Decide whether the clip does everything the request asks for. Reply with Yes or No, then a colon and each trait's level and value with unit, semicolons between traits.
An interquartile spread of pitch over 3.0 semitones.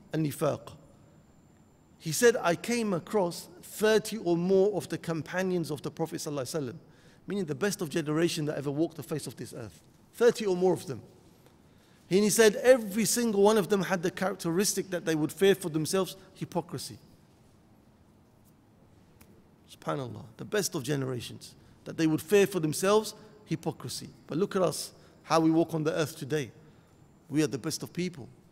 Yes: average, 4.0 semitones